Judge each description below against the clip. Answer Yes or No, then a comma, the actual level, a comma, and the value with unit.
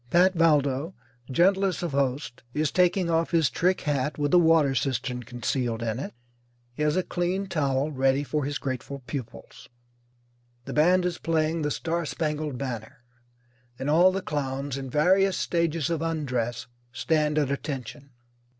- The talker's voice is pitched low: No, medium, 150 Hz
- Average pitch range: Yes, average, 3.9 semitones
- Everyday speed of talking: Yes, average, 155 wpm